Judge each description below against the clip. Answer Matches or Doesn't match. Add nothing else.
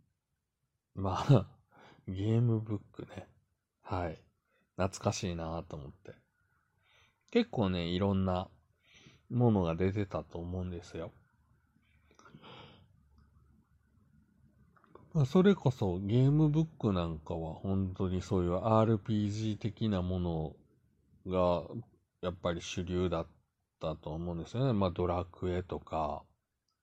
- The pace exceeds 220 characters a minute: Doesn't match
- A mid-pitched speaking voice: Doesn't match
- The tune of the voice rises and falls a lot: Doesn't match